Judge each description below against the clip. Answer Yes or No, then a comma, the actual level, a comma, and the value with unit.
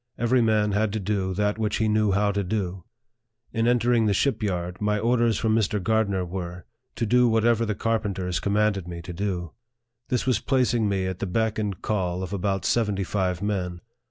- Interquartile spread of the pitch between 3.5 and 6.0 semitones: No, average, 3.1 semitones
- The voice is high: No, low, 105 Hz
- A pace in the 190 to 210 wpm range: Yes, average, 195 wpm